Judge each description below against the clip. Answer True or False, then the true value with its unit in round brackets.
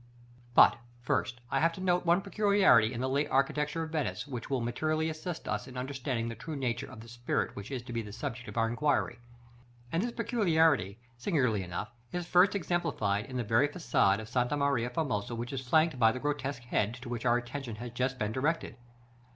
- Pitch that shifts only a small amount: False (4.9 semitones)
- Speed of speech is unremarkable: False (215 wpm)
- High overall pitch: False (130 Hz)